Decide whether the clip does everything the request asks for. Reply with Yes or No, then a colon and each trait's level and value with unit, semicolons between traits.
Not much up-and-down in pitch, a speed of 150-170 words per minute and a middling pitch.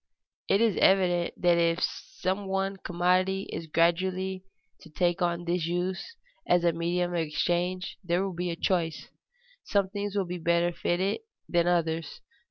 Yes: narrow, 1.7 semitones; average, 165 wpm; medium, 175 Hz